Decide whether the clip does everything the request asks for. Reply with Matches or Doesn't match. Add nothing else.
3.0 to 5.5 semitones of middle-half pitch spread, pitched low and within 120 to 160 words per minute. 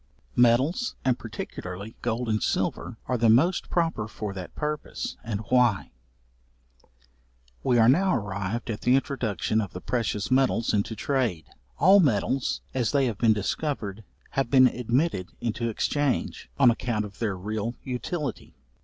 Matches